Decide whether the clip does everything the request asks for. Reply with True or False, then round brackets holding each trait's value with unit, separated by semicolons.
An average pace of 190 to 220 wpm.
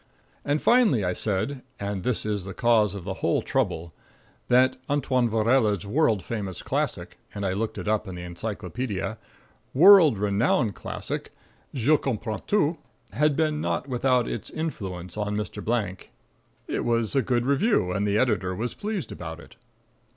False (160 wpm)